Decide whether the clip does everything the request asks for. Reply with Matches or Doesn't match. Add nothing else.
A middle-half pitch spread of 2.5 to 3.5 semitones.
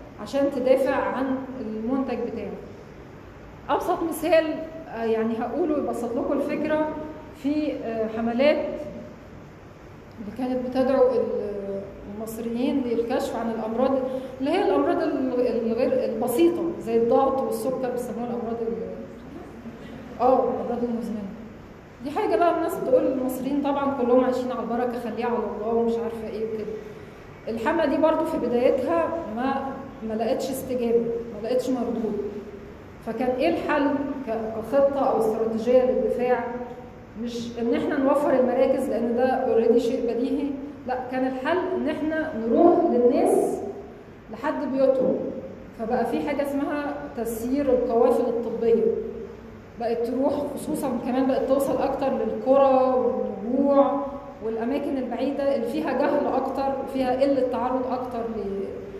Matches